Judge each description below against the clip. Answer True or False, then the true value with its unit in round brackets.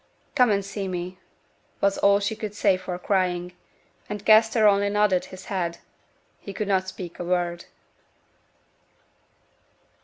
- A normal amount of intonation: False (2.3 semitones)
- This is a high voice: True (195 Hz)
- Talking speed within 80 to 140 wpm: True (135 wpm)